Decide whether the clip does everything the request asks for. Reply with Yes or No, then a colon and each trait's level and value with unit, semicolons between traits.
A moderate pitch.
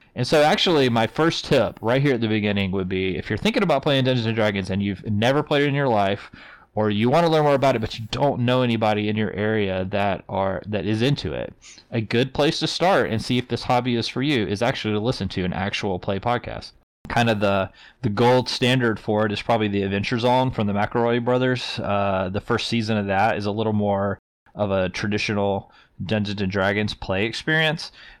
No: low, 110 Hz